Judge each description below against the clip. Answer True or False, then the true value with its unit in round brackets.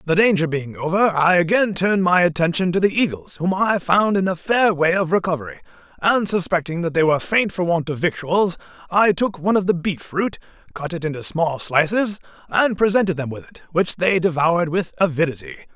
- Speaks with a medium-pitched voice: True (175 Hz)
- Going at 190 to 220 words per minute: True (200 wpm)